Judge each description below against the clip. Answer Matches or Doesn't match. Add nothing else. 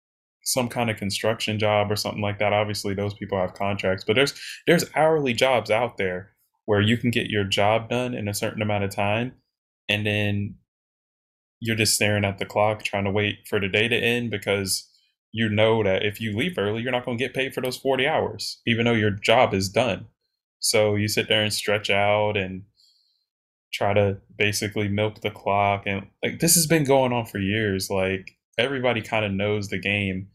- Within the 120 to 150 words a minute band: Doesn't match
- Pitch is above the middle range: Doesn't match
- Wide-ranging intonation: Doesn't match